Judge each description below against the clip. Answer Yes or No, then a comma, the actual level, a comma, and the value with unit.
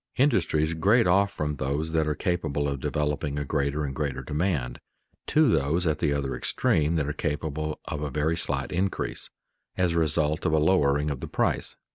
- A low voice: Yes, very low, 75 Hz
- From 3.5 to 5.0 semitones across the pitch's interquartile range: No, narrow, 2.5 semitones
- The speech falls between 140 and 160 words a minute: No, average, 190 wpm